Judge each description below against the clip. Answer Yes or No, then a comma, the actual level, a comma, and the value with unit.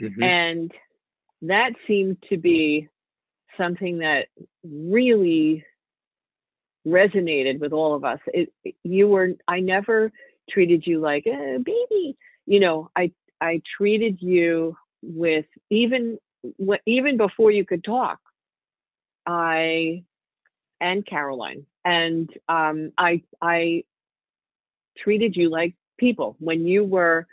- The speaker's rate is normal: No, slow, 110 wpm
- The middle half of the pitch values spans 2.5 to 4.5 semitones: Yes, average, 4.1 semitones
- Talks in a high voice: No, medium, 175 Hz